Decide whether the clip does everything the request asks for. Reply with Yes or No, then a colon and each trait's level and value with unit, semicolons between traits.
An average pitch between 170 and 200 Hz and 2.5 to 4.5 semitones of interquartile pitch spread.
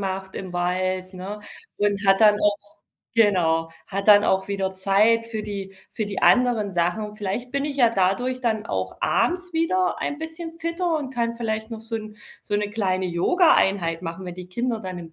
No: high, 210 Hz; average, 4.1 semitones